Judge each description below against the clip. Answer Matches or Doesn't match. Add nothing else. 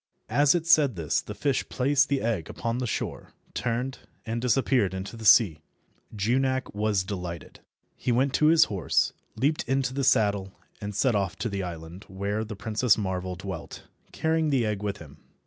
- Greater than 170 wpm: Matches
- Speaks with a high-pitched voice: Doesn't match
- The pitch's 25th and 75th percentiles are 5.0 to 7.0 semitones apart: Matches